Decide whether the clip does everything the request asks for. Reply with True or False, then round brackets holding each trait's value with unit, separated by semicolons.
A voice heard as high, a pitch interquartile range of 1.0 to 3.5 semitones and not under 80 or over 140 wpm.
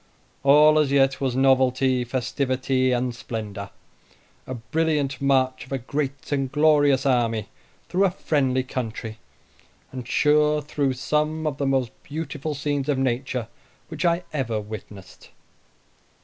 False (135 Hz; 2.8 semitones; 135 wpm)